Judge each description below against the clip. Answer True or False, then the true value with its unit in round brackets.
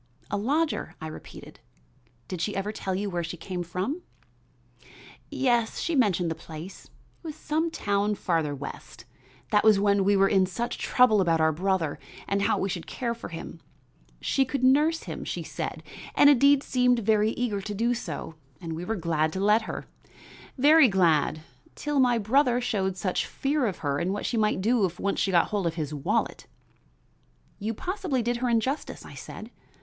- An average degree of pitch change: False (5.7 semitones)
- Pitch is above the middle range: True (205 Hz)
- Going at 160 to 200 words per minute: True (190 wpm)